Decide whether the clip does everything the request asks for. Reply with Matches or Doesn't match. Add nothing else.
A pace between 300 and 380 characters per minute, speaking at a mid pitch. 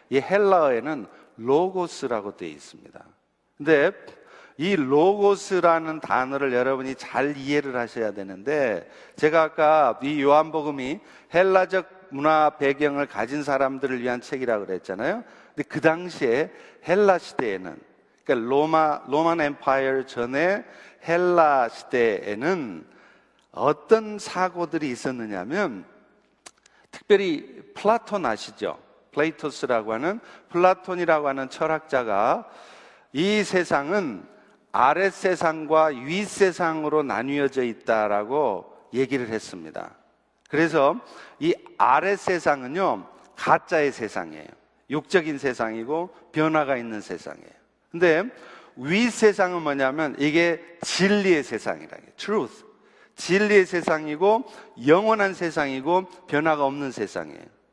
Doesn't match